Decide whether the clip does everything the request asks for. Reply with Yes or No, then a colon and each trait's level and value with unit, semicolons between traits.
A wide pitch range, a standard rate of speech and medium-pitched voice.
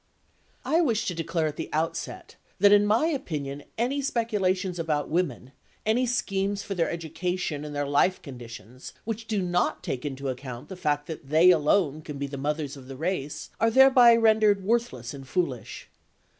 Yes: wide, 6.3 semitones; average, 175 wpm; medium, 170 Hz